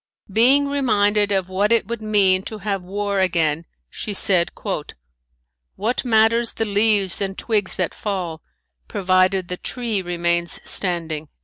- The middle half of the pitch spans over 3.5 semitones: No, average, 3.2 semitones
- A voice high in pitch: Yes, high, 200 Hz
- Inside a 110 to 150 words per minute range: Yes, slow, 135 wpm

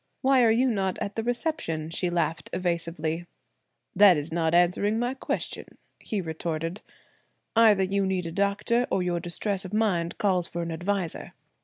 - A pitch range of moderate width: Yes, average, 3.7 semitones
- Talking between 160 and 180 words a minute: Yes, average, 165 wpm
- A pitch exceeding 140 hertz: Yes, medium, 185 Hz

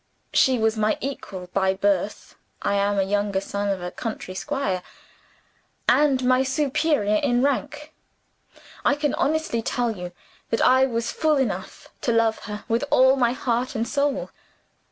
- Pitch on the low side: No, high, 235 Hz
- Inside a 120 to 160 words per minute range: Yes, average, 155 wpm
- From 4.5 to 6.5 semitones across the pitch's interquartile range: Yes, average, 5.1 semitones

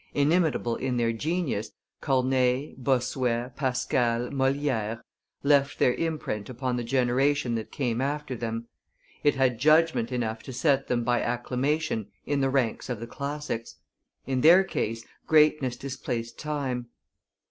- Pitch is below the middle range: Yes, low, 130 Hz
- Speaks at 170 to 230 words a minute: No, slow, 135 wpm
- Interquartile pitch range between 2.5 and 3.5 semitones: Yes, average, 3.1 semitones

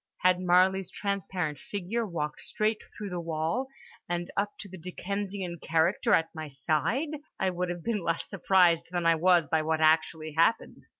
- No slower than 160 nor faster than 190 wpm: Yes, average, 170 wpm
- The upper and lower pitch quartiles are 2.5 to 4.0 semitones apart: Yes, average, 3.3 semitones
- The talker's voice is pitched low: No, medium, 175 Hz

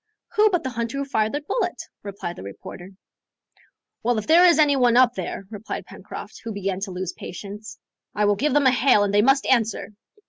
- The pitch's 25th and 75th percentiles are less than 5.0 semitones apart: No, average, 5.3 semitones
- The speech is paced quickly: Yes, fast, 210 wpm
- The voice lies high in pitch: Yes, high, 230 Hz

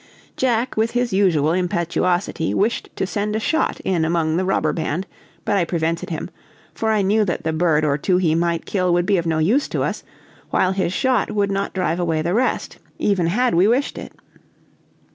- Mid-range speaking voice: Yes, medium, 180 Hz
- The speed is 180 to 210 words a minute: Yes, average, 200 wpm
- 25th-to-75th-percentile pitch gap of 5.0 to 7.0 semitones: No, average, 3.9 semitones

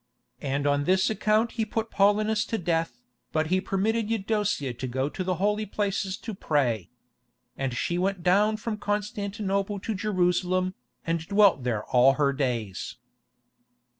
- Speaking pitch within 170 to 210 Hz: Yes, medium, 185 Hz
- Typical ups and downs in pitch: No, wide, 6.5 semitones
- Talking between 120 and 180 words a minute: Yes, average, 150 wpm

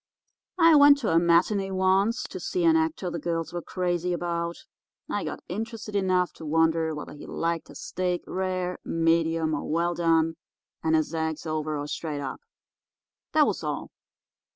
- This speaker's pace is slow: No, average, 170 wpm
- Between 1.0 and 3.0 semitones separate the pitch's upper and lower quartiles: Yes, narrow, 2.6 semitones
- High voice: No, medium, 170 Hz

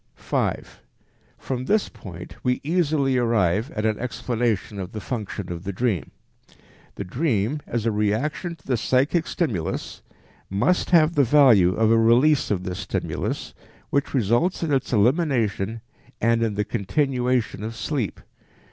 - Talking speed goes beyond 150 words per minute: No, average, 145 wpm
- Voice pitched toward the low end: Yes, low, 115 Hz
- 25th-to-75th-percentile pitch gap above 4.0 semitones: Yes, average, 5.1 semitones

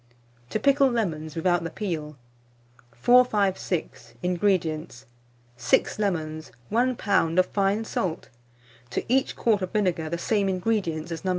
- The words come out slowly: Yes, slow, 130 wpm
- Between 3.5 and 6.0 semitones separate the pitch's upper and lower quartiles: Yes, average, 4.9 semitones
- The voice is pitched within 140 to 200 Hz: Yes, medium, 185 Hz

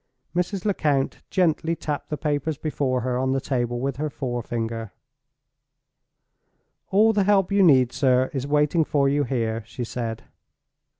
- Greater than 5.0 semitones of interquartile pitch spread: No, average, 4.3 semitones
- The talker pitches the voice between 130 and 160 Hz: Yes, medium, 140 Hz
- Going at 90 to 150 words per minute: Yes, average, 145 wpm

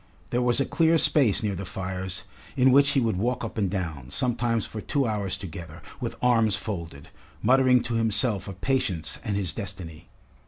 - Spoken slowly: No, average, 185 wpm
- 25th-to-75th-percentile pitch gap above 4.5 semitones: Yes, average, 5.0 semitones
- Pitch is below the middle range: Yes, low, 105 Hz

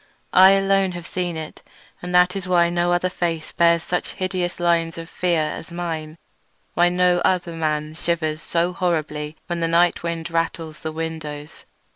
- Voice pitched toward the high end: No, medium, 170 Hz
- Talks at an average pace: Yes, average, 170 wpm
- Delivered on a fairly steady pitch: Yes, narrow, 1.6 semitones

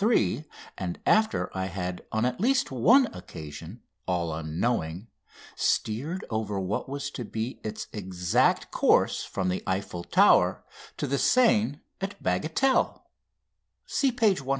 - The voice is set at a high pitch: No, low, 110 Hz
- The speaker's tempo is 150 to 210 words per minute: No, slow, 135 wpm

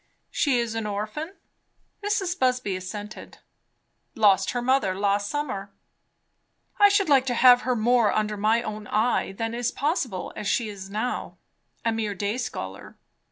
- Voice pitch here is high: Yes, high, 225 Hz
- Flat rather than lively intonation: No, average, 3.8 semitones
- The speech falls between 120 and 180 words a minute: Yes, average, 155 wpm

